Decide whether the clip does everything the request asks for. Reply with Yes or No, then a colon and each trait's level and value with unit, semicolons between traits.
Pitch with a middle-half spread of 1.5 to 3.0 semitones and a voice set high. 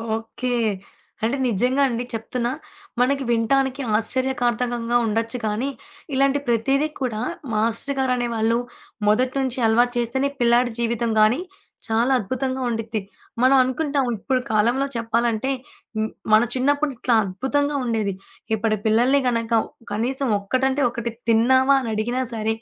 Yes: average, 2.7 semitones; high, 240 Hz